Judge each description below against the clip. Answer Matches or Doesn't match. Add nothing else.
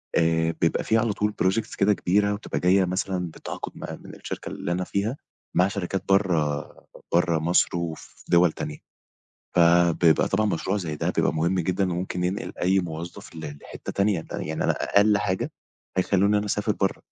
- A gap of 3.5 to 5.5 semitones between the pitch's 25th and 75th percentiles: Doesn't match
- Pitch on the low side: Matches